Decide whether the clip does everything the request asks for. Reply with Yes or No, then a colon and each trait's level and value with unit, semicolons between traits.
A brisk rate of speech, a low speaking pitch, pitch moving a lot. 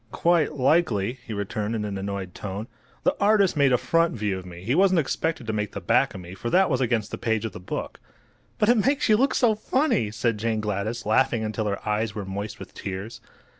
Yes: fast, 230 wpm; low, 115 Hz; wide, 7.2 semitones